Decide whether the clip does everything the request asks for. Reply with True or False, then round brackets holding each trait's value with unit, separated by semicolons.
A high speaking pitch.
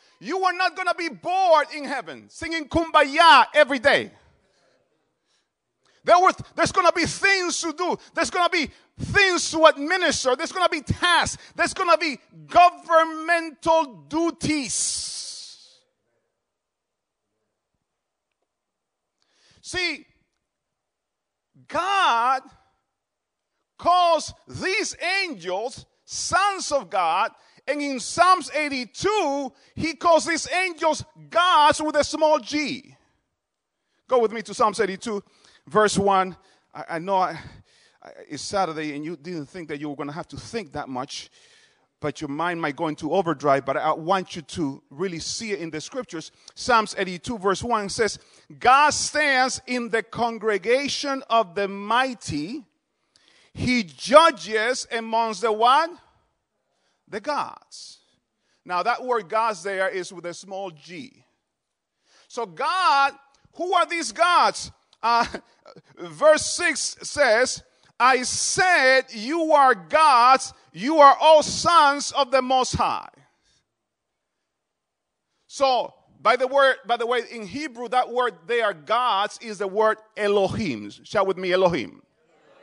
True (255 Hz)